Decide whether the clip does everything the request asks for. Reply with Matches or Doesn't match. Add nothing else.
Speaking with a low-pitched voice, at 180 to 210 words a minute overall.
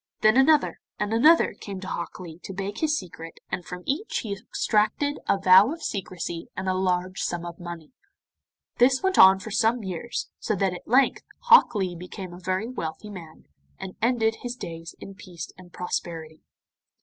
Doesn't match